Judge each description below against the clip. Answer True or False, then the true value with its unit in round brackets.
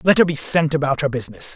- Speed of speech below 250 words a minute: False (270 wpm)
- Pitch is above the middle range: False (150 Hz)